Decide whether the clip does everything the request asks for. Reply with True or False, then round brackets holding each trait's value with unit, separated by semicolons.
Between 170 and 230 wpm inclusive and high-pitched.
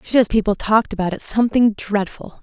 True (200 wpm; 215 Hz)